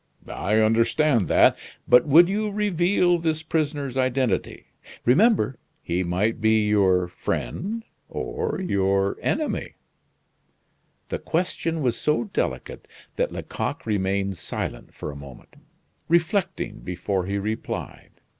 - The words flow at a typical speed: No, slow, 115 wpm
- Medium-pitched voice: No, low, 120 Hz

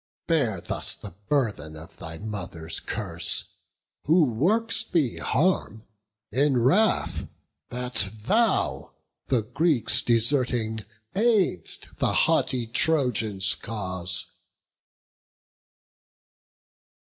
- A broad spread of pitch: Yes, wide, 6.6 semitones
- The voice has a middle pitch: No, low, 120 Hz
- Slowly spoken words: Yes, slow, 85 wpm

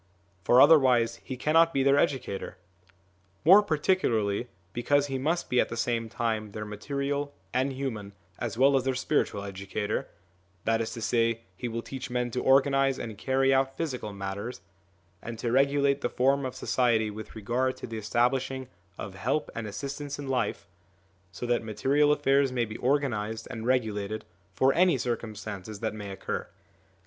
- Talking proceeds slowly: No, average, 165 wpm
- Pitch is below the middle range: Yes, low, 125 Hz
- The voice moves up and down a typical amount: Yes, average, 3.7 semitones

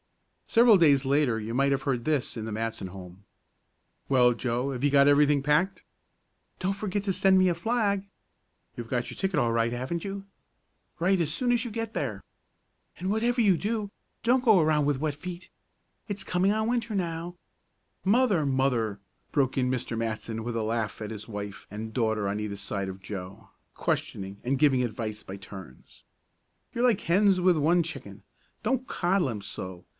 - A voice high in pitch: No, medium, 140 Hz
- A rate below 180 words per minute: No, average, 185 wpm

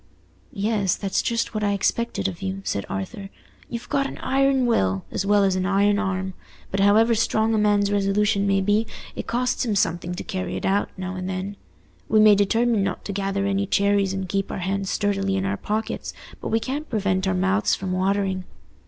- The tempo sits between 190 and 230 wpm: Yes, fast, 205 wpm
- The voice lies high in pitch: Yes, high, 200 Hz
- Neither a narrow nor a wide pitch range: No, narrow, 2.0 semitones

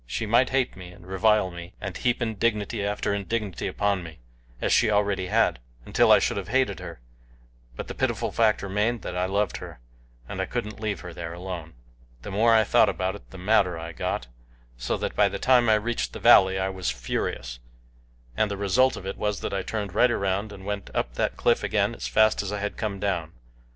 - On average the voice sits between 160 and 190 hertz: No, low, 100 Hz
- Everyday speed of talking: No, fast, 215 wpm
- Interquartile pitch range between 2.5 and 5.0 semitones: Yes, average, 2.8 semitones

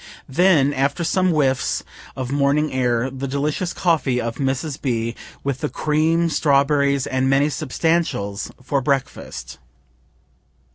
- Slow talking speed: Yes, slow, 125 wpm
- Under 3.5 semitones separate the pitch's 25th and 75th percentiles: Yes, average, 2.8 semitones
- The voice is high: No, medium, 140 Hz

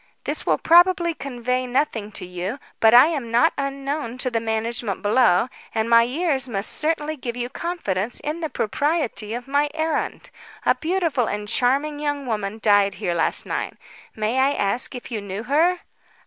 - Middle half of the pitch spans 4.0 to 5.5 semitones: Yes, average, 5.2 semitones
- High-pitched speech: Yes, very high, 250 Hz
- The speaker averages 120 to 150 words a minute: No, average, 175 wpm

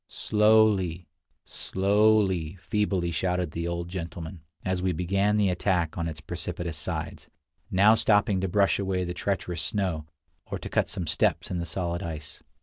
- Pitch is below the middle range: Yes, very low, 90 Hz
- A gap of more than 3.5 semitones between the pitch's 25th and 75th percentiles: No, average, 2.7 semitones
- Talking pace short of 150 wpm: No, average, 155 wpm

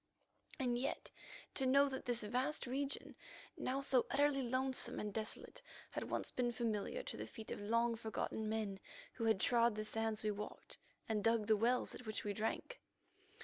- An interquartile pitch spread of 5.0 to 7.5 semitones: No, average, 3.2 semitones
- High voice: Yes, high, 230 Hz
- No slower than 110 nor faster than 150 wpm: No, average, 180 wpm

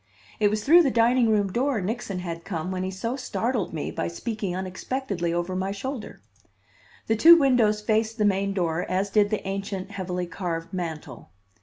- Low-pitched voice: No, high, 200 Hz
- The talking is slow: No, average, 180 wpm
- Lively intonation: No, average, 3.7 semitones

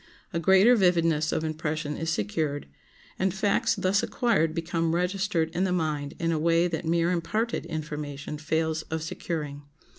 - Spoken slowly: No, average, 155 wpm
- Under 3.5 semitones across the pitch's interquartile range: Yes, narrow, 2.4 semitones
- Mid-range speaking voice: Yes, medium, 165 Hz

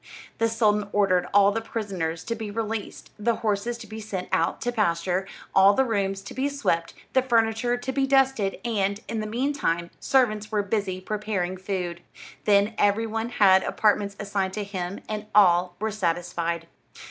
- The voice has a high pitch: Yes, high, 205 Hz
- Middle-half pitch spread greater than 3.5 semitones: No, average, 3.1 semitones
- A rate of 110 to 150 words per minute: No, average, 170 wpm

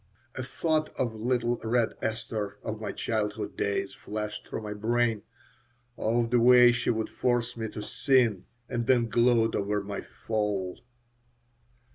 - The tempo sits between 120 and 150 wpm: Yes, average, 145 wpm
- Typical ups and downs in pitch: No, narrow, 2.3 semitones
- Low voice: Yes, low, 115 Hz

